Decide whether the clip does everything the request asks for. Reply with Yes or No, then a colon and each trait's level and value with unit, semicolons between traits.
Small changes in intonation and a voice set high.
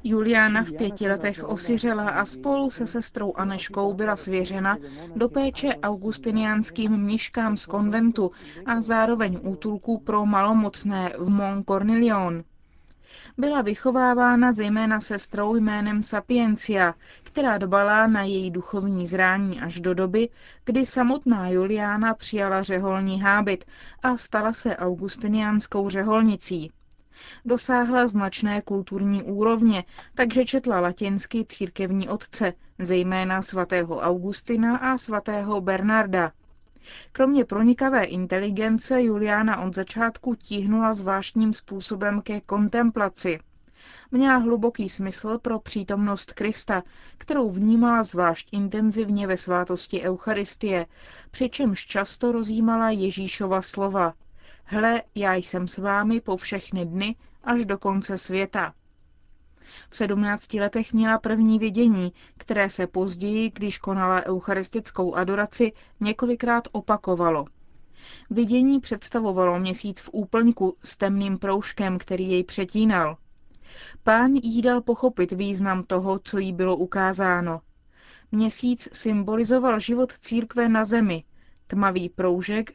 No: average, 3.0 semitones; high, 205 Hz